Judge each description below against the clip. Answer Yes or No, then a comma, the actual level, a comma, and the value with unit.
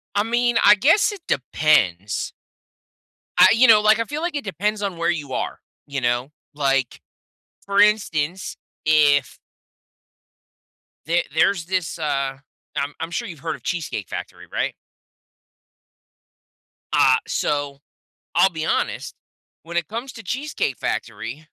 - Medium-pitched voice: Yes, medium, 165 Hz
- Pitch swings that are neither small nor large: No, wide, 6.8 semitones